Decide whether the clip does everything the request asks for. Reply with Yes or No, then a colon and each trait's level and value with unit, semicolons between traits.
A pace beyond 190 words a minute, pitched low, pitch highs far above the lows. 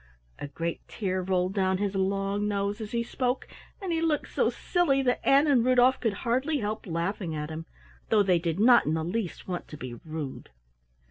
No: average, 200 wpm; high, 200 Hz; wide, 5.9 semitones